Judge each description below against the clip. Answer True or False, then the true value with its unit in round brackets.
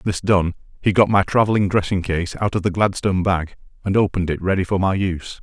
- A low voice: True (95 Hz)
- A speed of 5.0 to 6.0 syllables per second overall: False (6.2 syllables/s)